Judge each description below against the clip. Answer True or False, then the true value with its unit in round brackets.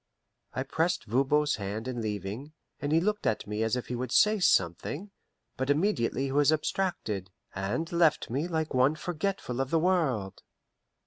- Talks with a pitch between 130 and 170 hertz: True (140 Hz)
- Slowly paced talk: False (170 wpm)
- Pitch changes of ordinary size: False (6.5 semitones)